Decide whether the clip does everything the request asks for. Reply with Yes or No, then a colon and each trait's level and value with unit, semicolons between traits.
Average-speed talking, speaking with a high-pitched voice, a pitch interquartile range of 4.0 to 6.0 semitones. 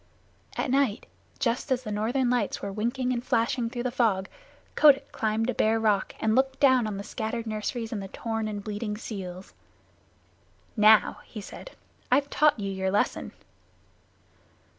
No: average, 160 wpm; high, 225 Hz; average, 3.2 semitones